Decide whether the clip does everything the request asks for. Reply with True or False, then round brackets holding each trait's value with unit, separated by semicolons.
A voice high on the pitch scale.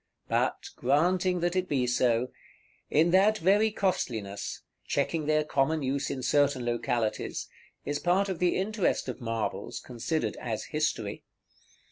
False (150 Hz)